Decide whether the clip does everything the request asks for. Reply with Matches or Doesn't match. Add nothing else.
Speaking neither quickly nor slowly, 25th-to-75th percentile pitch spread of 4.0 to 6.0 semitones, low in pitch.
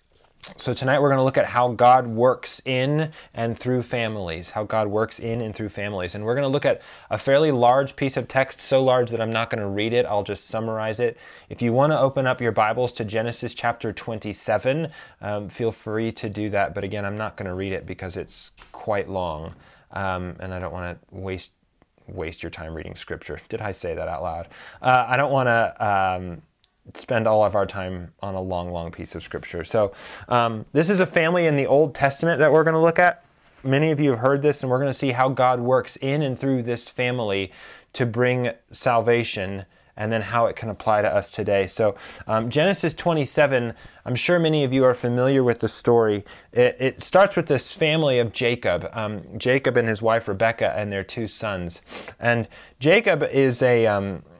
Doesn't match